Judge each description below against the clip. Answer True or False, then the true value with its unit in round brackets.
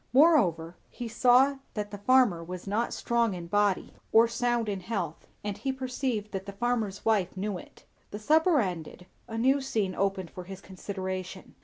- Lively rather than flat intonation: False (4.3 semitones)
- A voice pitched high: True (205 Hz)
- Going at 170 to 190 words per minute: True (175 wpm)